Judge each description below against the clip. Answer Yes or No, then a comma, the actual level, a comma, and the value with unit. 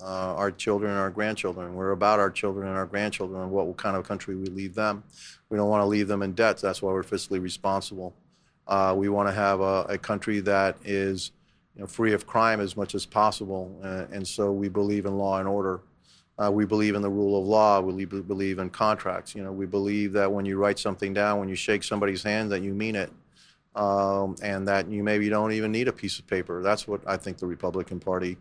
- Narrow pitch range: Yes, narrow, 1.4 semitones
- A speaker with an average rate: No, fast, 240 wpm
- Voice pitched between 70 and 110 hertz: Yes, low, 100 Hz